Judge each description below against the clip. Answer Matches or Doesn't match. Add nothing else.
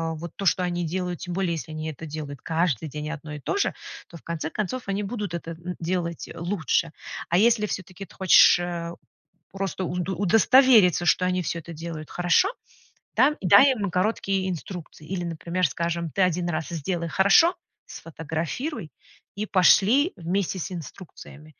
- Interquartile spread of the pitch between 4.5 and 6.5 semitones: Doesn't match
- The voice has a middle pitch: Matches